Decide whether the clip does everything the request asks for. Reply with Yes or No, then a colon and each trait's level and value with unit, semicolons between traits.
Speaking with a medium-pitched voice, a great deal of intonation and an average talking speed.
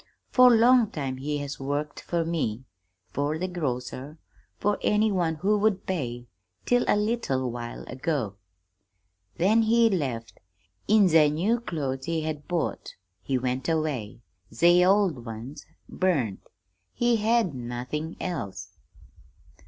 No: medium, 155 Hz; wide, 7.1 semitones; slow, 130 wpm